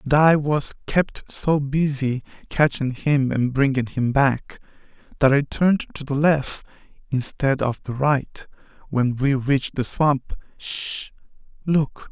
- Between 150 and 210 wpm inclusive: No, slow, 135 wpm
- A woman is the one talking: No, male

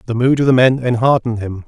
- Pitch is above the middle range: No, low, 120 Hz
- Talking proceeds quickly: Yes, fast, 250 wpm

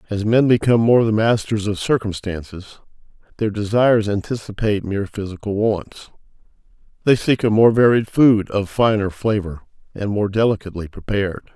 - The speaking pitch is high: No, low, 105 Hz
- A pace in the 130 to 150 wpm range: Yes, average, 140 wpm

